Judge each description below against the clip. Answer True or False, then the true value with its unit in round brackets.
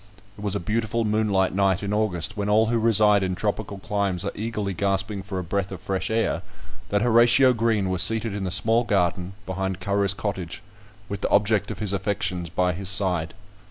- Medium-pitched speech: False (100 Hz)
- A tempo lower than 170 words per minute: False (195 wpm)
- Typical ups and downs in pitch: False (2.3 semitones)